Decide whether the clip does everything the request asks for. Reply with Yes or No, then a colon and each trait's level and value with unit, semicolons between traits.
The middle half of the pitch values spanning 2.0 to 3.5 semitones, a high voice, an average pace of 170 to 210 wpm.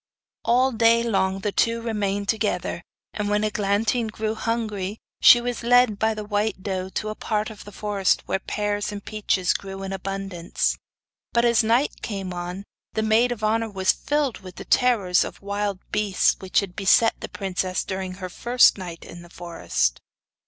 Yes: average, 2.8 semitones; high, 205 Hz; average, 180 wpm